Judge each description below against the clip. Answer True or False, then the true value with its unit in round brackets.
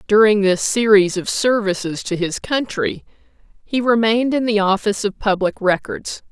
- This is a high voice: True (210 Hz)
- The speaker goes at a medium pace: True (150 wpm)